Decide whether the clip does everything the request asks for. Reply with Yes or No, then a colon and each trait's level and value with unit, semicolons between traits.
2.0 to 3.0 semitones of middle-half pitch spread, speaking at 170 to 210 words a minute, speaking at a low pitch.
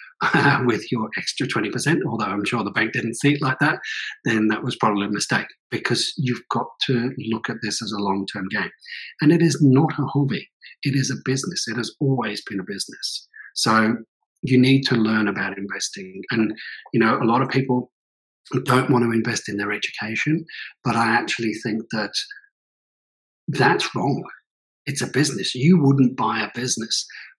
No: average, 3.8 semitones; average, 185 wpm; low, 120 Hz